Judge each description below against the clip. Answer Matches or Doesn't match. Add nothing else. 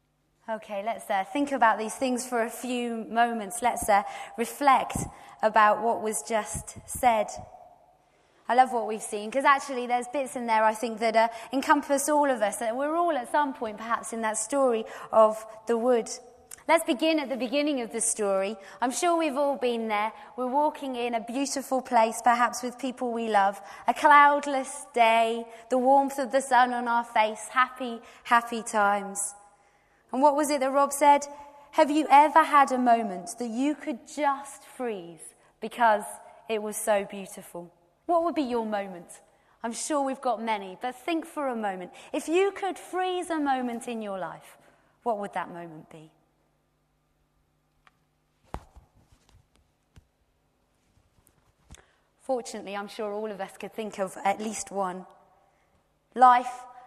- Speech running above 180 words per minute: Doesn't match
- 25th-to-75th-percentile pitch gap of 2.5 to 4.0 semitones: Doesn't match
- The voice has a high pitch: Matches